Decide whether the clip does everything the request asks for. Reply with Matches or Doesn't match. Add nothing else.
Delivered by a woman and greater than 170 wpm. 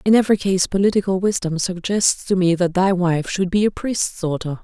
Matches